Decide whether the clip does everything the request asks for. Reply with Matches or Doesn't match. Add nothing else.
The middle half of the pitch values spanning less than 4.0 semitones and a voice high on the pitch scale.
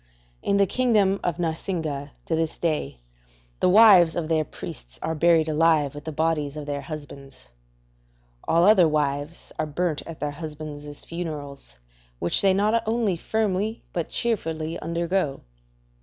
Doesn't match